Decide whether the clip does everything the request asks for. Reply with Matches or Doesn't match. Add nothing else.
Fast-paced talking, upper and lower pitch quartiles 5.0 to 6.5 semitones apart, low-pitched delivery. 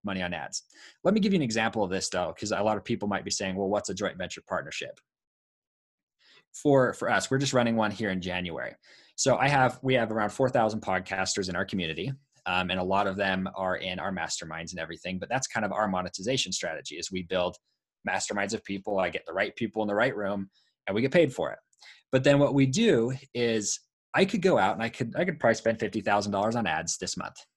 Matches